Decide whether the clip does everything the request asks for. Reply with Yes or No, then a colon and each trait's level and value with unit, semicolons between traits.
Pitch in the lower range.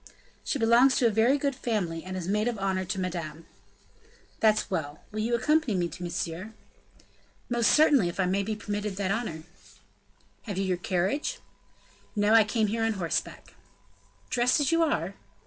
No: high, 210 Hz